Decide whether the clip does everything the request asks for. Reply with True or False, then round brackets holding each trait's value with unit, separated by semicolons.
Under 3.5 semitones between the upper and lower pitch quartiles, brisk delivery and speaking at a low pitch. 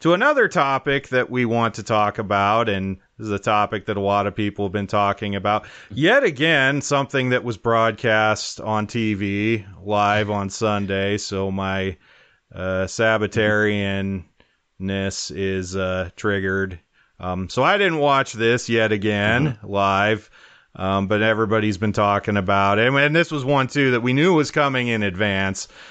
False (3.0 semitones; 160 wpm; 105 Hz)